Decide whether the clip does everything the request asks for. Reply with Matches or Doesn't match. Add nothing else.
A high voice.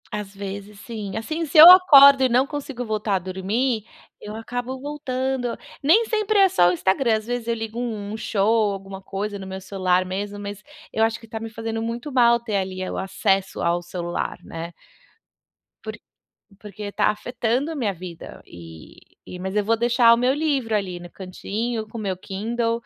Matches